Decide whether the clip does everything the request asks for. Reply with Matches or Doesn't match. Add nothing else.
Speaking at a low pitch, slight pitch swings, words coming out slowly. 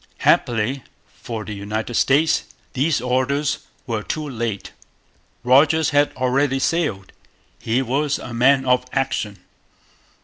Doesn't match